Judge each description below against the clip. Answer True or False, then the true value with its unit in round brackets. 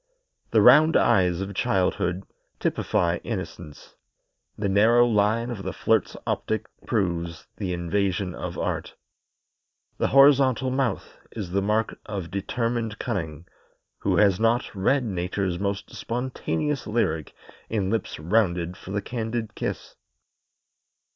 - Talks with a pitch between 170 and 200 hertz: False (100 Hz)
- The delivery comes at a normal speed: False (120 wpm)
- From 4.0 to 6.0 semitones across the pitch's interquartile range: True (4.5 semitones)